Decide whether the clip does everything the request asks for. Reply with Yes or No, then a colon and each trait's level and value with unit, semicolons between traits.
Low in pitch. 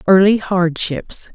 No: medium, 185 Hz